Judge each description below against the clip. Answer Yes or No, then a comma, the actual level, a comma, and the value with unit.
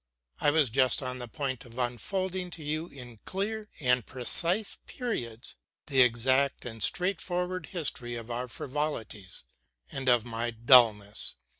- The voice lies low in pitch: Yes, low, 130 Hz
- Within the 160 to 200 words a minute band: No, average, 140 wpm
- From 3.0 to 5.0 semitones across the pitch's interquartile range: No, wide, 5.6 semitones